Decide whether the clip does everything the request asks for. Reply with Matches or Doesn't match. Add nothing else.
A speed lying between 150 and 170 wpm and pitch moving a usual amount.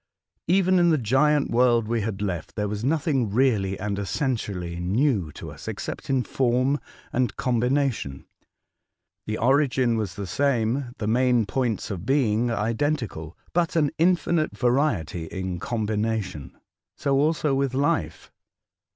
Doesn't match